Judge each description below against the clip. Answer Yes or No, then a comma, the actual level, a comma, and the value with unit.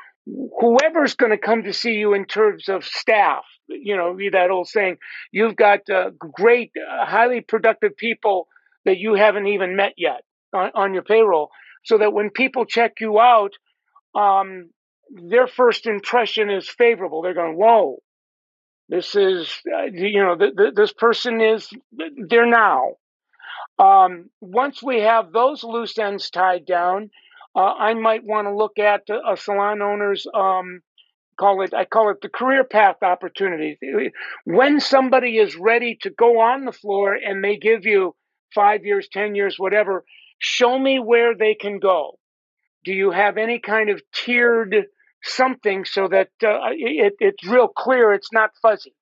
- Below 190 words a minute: Yes, average, 165 wpm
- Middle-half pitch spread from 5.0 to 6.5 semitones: No, average, 3.5 semitones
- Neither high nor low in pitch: No, high, 215 Hz